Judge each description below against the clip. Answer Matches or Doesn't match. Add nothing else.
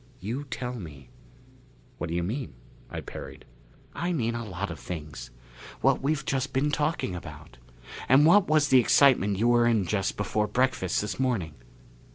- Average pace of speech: Matches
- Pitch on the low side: Matches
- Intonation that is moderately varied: Doesn't match